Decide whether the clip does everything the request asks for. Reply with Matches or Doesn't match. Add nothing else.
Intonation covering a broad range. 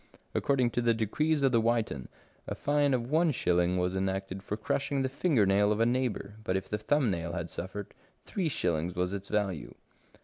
Matches